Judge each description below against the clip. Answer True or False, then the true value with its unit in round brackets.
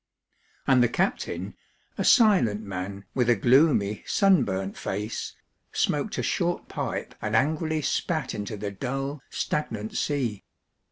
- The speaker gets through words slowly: True (125 wpm)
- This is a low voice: True (120 Hz)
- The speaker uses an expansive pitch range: True (6.5 semitones)